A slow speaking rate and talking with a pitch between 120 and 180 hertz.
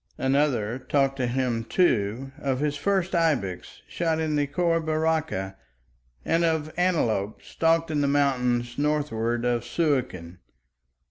Yes: slow, 130 wpm; medium, 140 Hz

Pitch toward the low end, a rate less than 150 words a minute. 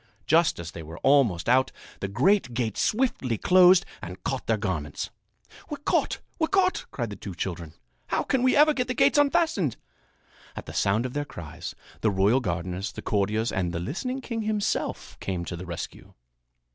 No: low, 120 Hz; average, 185 wpm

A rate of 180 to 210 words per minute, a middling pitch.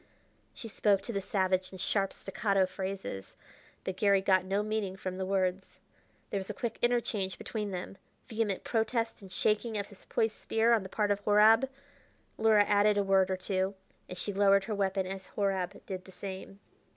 No: average, 190 wpm; high, 195 Hz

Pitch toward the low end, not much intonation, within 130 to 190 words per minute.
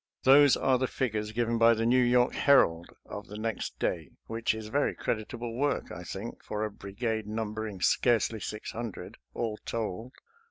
Yes: low, 115 Hz; narrow, 2.2 semitones; average, 170 wpm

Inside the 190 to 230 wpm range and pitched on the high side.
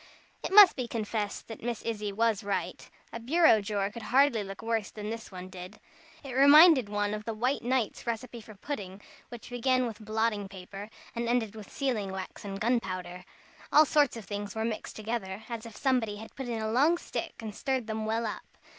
Yes: fast, 205 wpm; high, 220 Hz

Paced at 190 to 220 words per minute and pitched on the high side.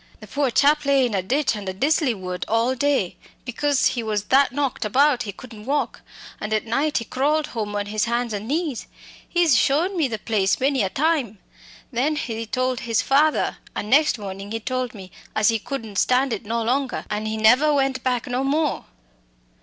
Yes: average, 200 wpm; very high, 250 Hz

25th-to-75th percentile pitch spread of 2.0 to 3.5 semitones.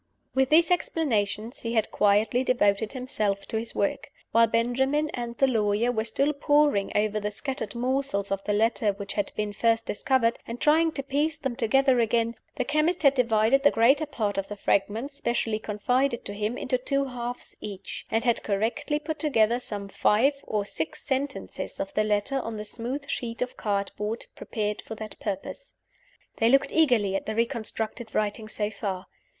No: average, 4.2 semitones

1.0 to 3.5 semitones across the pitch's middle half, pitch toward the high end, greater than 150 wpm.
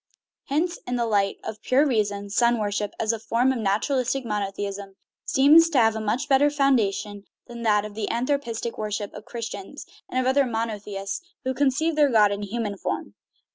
No: average, 4.3 semitones; high, 230 Hz; average, 175 wpm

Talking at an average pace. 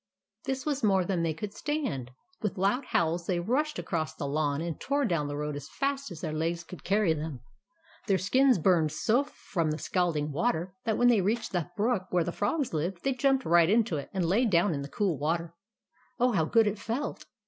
No: fast, 215 wpm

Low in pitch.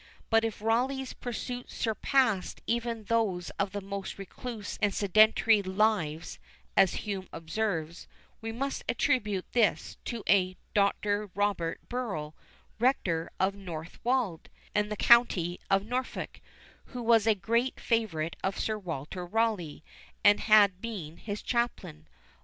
No: high, 205 Hz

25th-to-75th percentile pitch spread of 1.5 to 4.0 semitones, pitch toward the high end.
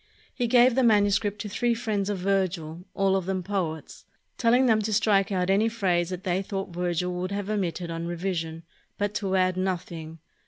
Yes: average, 2.7 semitones; high, 195 Hz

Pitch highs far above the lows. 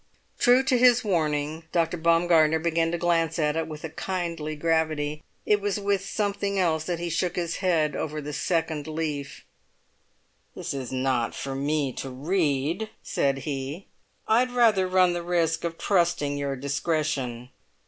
No: average, 3.3 semitones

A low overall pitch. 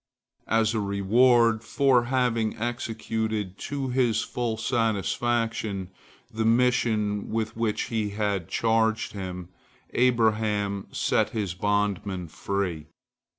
Yes: low, 110 Hz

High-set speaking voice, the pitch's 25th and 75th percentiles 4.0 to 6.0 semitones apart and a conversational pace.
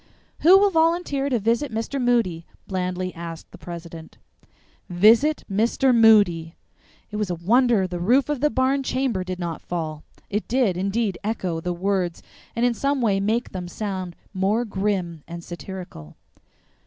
Yes: high, 200 Hz; wide, 5.5 semitones; average, 155 wpm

